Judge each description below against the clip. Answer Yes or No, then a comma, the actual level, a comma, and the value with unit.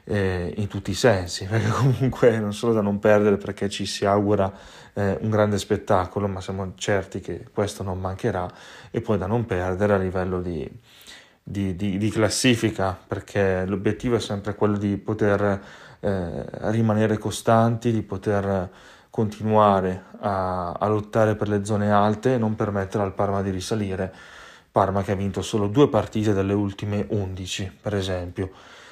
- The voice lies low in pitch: Yes, low, 100 Hz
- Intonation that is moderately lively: No, narrow, 1.9 semitones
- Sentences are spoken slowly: No, average, 155 wpm